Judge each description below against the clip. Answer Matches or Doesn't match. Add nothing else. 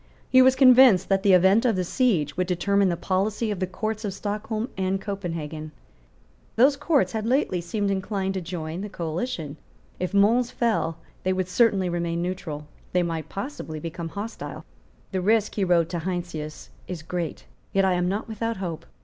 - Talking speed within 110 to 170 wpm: Doesn't match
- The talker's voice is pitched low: Doesn't match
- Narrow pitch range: Doesn't match